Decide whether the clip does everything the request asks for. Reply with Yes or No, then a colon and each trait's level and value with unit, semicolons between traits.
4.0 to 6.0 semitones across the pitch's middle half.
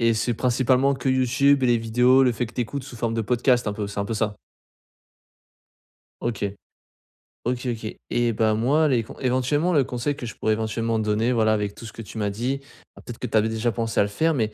No: average, 2.7 semitones